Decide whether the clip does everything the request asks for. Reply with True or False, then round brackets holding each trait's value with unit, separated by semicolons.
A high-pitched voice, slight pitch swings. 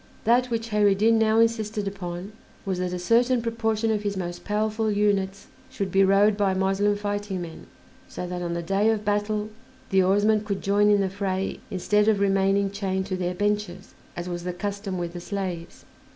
True (200 Hz; 2.0 semitones)